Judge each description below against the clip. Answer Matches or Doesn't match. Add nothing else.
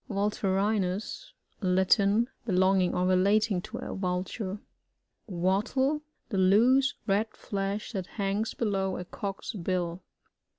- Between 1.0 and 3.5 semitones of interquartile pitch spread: Matches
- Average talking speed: Doesn't match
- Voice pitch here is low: Doesn't match